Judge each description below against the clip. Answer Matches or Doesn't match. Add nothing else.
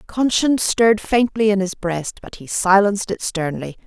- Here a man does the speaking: Doesn't match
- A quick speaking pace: Doesn't match